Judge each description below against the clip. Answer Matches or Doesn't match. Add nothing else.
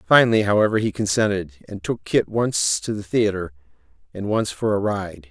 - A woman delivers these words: Doesn't match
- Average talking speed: Matches